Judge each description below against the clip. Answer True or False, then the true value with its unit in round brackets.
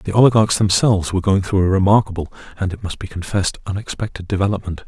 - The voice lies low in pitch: True (95 Hz)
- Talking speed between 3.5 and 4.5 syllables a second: False (6.8 syllables/s)